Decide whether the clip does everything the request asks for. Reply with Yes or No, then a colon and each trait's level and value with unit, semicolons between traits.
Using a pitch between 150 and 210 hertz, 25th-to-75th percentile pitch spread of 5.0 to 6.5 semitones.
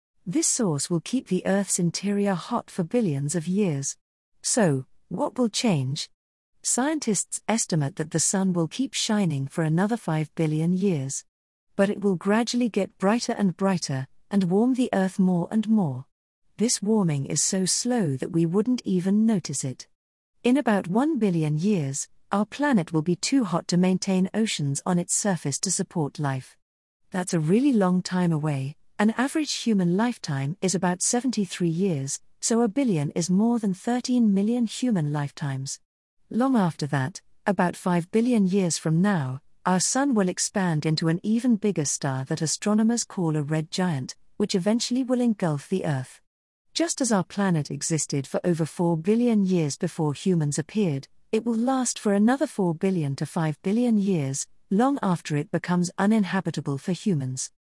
Yes: medium, 185 Hz; wide, 5.5 semitones